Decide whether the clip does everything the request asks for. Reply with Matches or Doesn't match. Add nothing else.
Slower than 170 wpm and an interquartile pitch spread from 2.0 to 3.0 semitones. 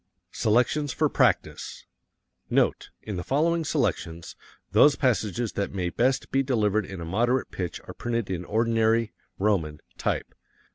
Doesn't match